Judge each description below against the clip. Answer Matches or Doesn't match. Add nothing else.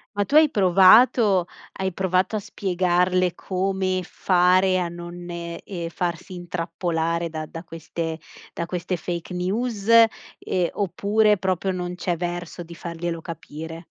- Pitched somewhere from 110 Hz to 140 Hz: Doesn't match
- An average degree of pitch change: Doesn't match